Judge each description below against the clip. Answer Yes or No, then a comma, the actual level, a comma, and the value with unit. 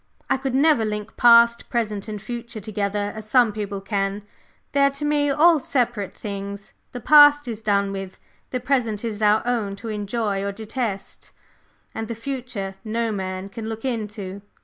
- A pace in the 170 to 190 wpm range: Yes, average, 175 wpm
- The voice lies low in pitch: No, high, 220 Hz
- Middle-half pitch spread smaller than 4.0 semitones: Yes, average, 3.4 semitones